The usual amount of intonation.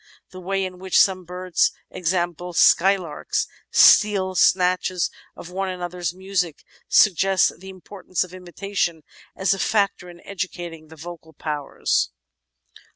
No: narrow, 1.6 semitones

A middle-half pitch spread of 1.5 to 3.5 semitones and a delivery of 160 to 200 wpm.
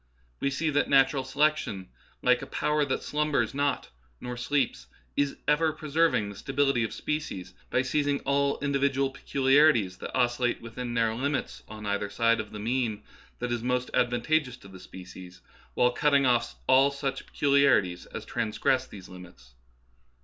No: average, 4.1 semitones; average, 165 wpm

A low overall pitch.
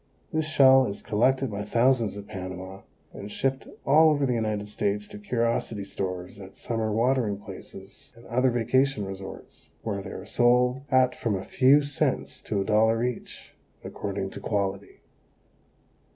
Yes: low, 110 Hz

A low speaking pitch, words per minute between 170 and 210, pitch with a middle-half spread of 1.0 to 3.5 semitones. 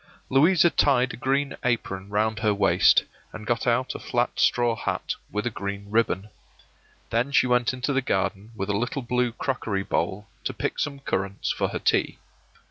No: low, 115 Hz; average, 180 wpm; average, 4.0 semitones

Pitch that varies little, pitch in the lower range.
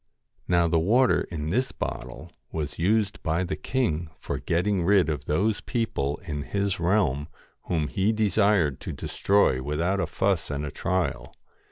No: average, 4.9 semitones; very low, 90 Hz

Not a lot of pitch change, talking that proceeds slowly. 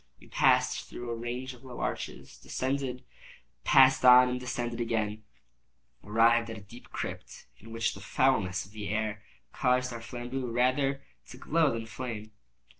No: narrow, 2.1 semitones; average, 160 wpm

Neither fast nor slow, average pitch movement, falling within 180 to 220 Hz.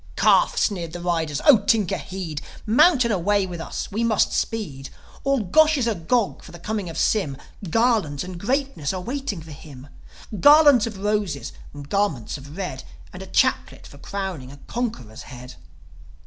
No: average, 175 wpm; wide, 6.6 semitones; high, 190 Hz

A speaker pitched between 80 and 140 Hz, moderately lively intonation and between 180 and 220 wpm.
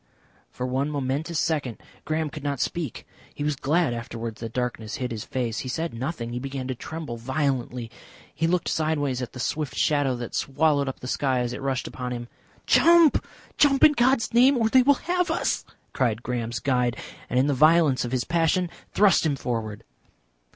Yes: low, 135 Hz; average, 4.7 semitones; average, 190 wpm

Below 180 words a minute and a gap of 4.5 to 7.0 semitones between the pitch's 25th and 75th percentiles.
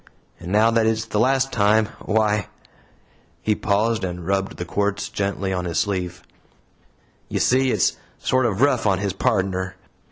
No: average, 160 wpm; average, 2.8 semitones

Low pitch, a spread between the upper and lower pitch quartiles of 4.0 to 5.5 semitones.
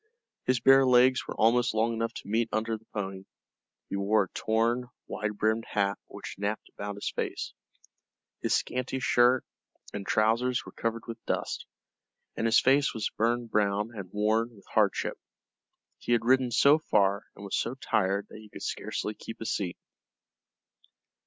No: low, 110 Hz; average, 2.8 semitones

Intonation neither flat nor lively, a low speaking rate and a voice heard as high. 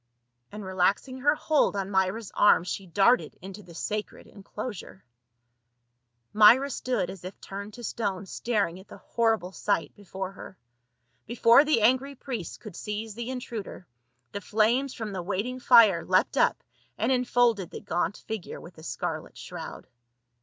No: average, 4.1 semitones; average, 155 wpm; high, 210 Hz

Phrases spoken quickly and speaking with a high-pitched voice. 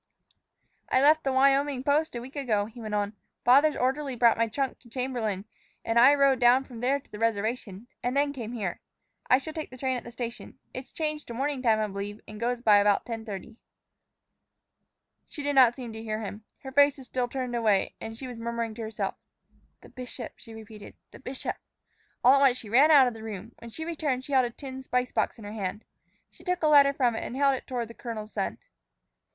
Yes: fast, 225 wpm; high, 245 Hz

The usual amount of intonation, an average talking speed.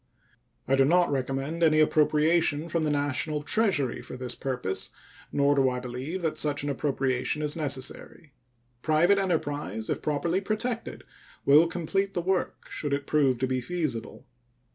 Yes: average, 3.9 semitones; average, 155 wpm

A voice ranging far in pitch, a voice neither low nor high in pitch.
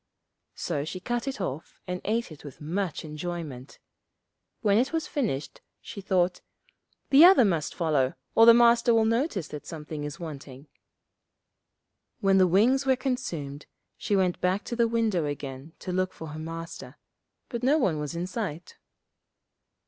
Yes: wide, 7.0 semitones; medium, 180 Hz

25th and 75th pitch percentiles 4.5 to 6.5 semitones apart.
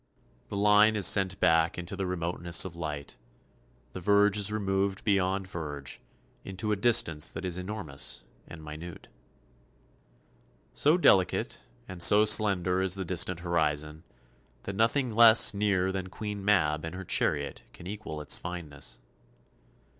No: average, 3.8 semitones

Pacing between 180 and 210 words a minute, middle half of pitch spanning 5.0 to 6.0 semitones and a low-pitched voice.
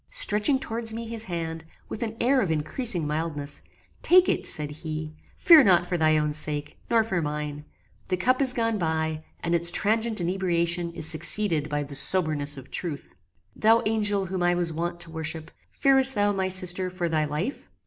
No: average, 185 wpm; wide, 5.6 semitones; medium, 175 Hz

